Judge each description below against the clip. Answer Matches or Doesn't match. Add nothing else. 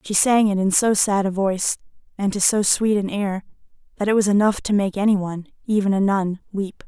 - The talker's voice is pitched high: Matches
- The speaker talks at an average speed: Doesn't match